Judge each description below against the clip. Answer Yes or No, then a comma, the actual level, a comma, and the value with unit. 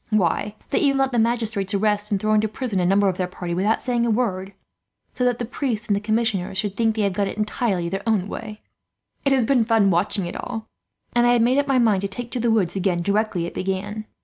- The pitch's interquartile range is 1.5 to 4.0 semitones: Yes, average, 3.3 semitones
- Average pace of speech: No, fast, 255 wpm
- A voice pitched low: No, high, 215 Hz